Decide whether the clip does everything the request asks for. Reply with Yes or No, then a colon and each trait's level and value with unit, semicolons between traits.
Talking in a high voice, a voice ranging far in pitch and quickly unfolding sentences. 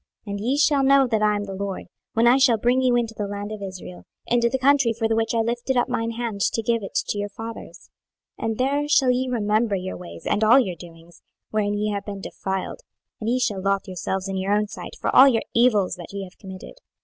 No: high, 220 Hz; average, 3.4 semitones; fast, 250 wpm